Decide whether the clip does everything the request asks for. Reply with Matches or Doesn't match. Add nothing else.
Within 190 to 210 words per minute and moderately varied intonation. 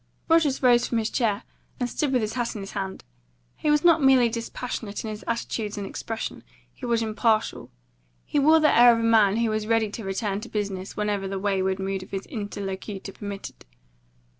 Matches